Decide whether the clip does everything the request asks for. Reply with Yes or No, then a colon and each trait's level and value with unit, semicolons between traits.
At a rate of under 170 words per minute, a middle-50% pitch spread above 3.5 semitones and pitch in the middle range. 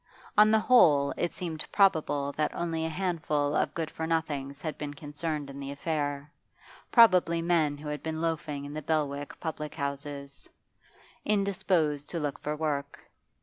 No: average, 160 wpm; narrow, 2.5 semitones; medium, 155 Hz